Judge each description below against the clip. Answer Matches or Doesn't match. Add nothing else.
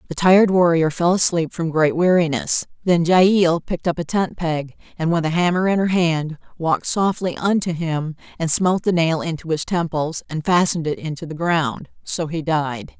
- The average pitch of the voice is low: Doesn't match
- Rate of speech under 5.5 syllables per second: Matches